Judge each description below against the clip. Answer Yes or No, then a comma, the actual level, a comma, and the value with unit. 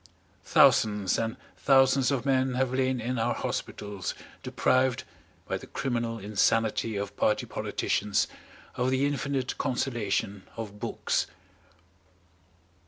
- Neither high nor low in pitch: No, low, 120 Hz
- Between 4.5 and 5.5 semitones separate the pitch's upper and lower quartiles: No, average, 3.7 semitones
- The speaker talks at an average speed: No, slow, 110 wpm